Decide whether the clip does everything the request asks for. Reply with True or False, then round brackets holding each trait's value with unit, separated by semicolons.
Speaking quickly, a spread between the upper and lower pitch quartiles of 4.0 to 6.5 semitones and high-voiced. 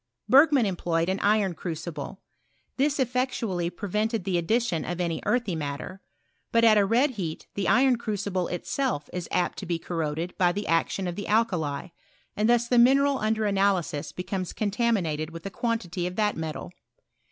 False (170 wpm; 5.0 semitones; 195 Hz)